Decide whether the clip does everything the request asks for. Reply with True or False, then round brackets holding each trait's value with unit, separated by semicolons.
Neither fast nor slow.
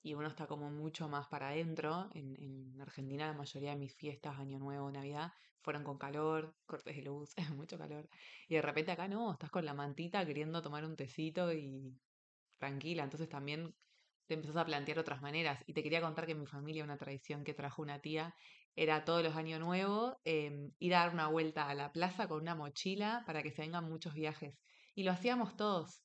False (210 wpm)